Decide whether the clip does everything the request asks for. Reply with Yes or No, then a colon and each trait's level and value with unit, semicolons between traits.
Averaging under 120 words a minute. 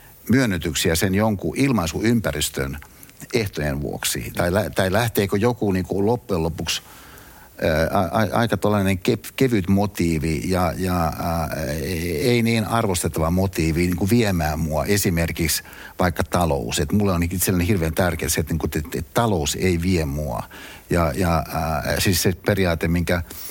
No: average, 145 wpm